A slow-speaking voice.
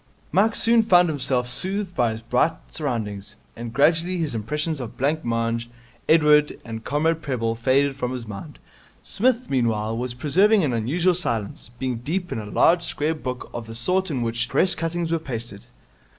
No: average, 170 wpm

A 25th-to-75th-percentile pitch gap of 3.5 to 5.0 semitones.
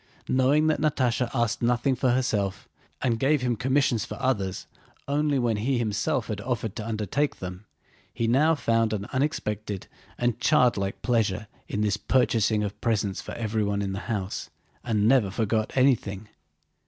Yes: average, 3.8 semitones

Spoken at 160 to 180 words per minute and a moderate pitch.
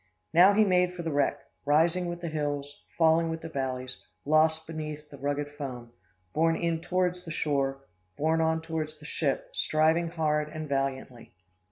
Yes: average, 170 wpm; medium, 155 Hz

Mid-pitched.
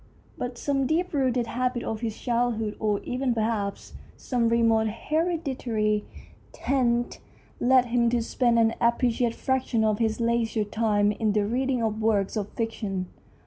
No: high, 230 Hz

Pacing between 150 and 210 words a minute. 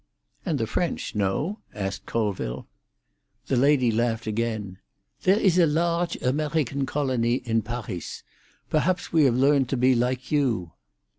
No: average, 140 wpm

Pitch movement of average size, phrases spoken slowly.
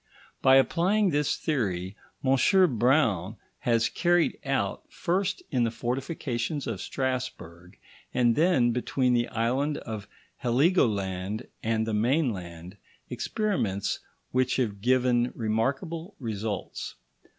Yes: average, 4.6 semitones; slow, 105 wpm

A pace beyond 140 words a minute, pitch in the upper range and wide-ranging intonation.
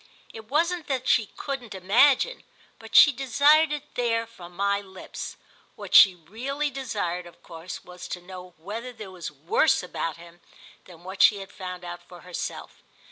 Yes: average, 170 wpm; high, 200 Hz; wide, 6.7 semitones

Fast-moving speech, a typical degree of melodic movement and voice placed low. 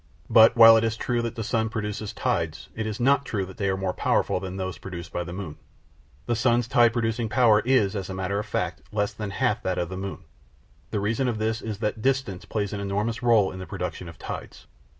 Yes: fast, 235 wpm; average, 3.2 semitones; low, 105 Hz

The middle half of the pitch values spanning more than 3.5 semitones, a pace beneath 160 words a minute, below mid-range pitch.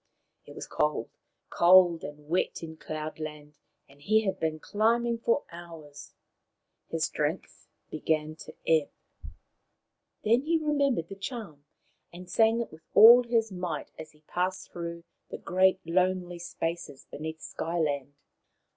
No: average, 4.8 semitones; average, 140 wpm; medium, 170 Hz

